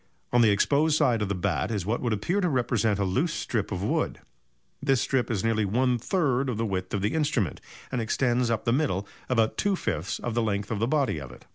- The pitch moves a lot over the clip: No, average, 4.4 semitones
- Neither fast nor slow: No, fast, 240 wpm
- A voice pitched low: Yes, low, 115 Hz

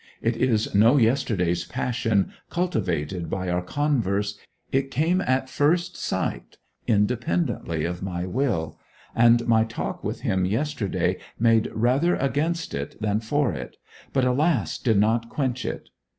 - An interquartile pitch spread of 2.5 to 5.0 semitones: No, wide, 5.6 semitones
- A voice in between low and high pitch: No, low, 115 Hz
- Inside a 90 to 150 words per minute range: Yes, slow, 135 wpm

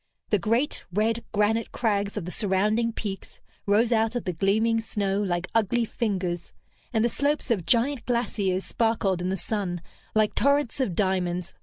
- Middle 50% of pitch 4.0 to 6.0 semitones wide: No, average, 3.3 semitones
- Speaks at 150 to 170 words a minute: Yes, average, 165 wpm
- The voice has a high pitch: Yes, high, 210 Hz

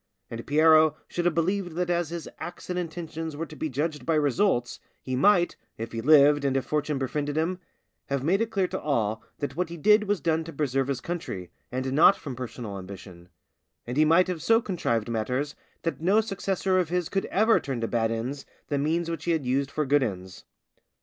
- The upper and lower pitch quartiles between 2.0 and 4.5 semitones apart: No, average, 5.0 semitones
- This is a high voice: No, medium, 150 Hz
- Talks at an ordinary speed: No, fast, 215 wpm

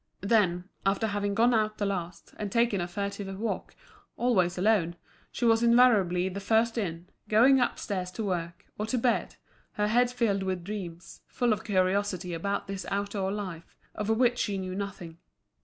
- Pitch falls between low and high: No, high, 200 Hz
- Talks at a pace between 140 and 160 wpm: No, average, 170 wpm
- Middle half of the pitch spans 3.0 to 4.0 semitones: Yes, average, 3.3 semitones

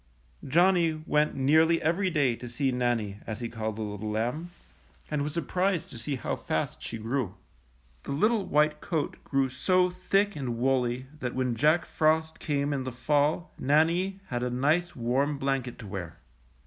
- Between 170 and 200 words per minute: Yes, average, 180 wpm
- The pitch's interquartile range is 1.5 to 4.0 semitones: No, average, 4.8 semitones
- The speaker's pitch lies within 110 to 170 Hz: Yes, medium, 140 Hz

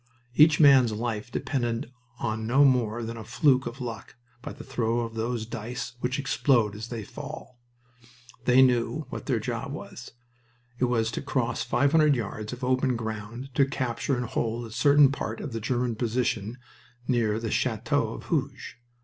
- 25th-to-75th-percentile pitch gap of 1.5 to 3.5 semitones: Yes, narrow, 2.4 semitones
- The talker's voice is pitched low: Yes, low, 120 Hz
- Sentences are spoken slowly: No, average, 175 wpm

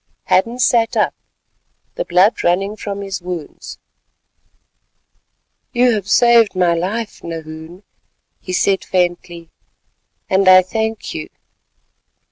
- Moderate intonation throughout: Yes, average, 4.0 semitones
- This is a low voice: No, high, 190 Hz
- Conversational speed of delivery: No, slow, 105 wpm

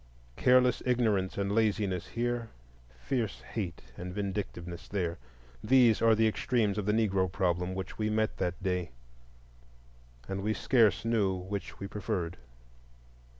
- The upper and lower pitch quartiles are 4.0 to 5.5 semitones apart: No, average, 3.6 semitones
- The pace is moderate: No, slow, 130 wpm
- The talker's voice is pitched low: Yes, low, 100 Hz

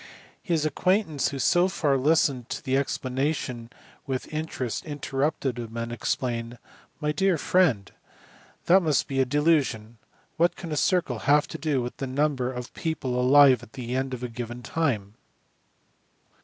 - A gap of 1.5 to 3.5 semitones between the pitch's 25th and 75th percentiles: No, average, 3.9 semitones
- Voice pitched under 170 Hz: Yes, low, 135 Hz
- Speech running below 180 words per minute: Yes, average, 170 wpm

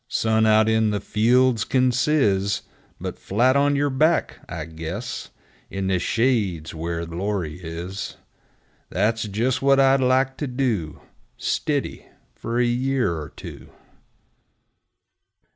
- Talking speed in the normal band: No, slow, 125 wpm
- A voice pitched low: Yes, low, 110 Hz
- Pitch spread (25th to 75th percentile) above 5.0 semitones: Yes, wide, 5.5 semitones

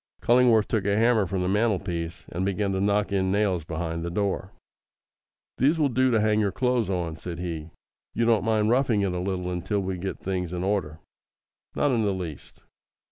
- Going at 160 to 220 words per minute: Yes, average, 195 wpm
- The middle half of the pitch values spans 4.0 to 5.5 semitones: No, average, 3.5 semitones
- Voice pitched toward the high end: No, low, 100 Hz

